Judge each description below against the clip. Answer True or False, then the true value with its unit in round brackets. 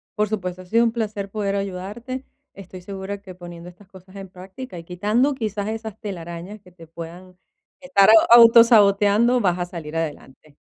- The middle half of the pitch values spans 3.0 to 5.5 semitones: True (3.4 semitones)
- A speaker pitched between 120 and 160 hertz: False (195 Hz)